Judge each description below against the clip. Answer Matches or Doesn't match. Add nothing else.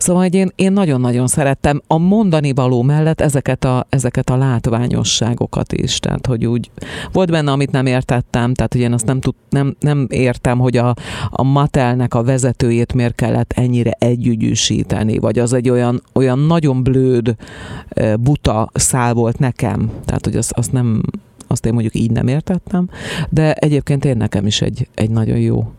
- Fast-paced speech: Matches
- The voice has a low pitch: Matches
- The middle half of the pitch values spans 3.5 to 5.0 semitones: Doesn't match